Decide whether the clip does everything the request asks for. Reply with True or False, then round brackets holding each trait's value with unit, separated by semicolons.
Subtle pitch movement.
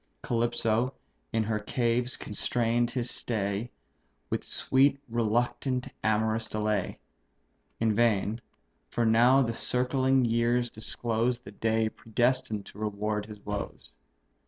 True (2.2 semitones)